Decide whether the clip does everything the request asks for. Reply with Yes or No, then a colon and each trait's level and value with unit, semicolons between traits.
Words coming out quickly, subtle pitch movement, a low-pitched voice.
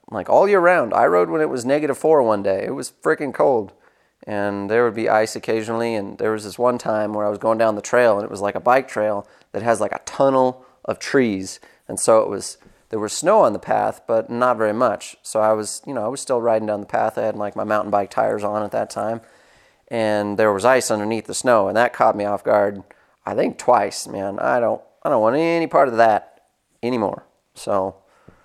Yes: fast, 245 wpm; narrow, 2.3 semitones; low, 110 Hz